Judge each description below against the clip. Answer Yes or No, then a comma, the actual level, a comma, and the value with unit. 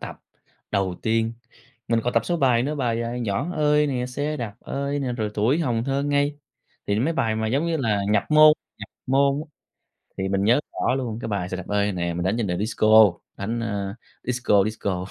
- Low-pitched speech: Yes, low, 115 Hz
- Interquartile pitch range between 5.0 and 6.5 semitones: Yes, average, 5.3 semitones